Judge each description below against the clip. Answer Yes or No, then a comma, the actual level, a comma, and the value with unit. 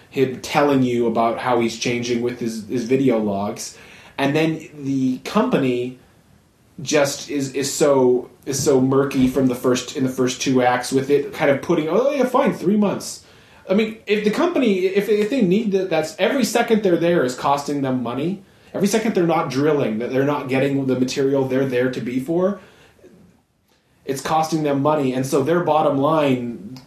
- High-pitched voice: No, medium, 140 Hz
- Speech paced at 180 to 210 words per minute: Yes, average, 190 wpm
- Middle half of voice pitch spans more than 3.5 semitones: Yes, average, 5.1 semitones